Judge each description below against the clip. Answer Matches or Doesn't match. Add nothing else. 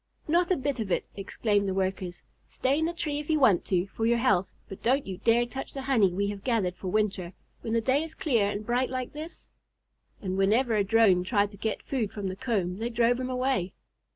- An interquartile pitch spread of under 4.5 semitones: Doesn't match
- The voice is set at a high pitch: Matches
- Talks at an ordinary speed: Doesn't match